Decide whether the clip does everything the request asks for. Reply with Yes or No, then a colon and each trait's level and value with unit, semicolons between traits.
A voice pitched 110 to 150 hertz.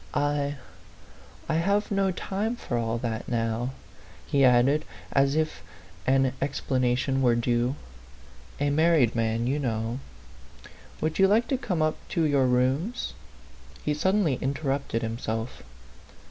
Yes: low, 135 Hz